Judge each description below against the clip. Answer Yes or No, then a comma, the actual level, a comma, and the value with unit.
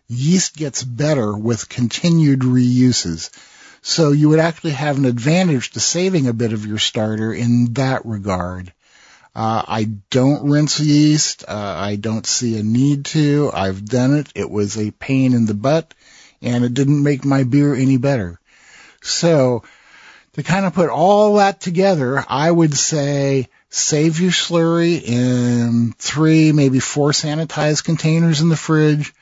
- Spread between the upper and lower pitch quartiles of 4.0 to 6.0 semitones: Yes, average, 4.8 semitones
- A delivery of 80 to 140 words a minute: No, average, 155 wpm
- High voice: No, medium, 140 Hz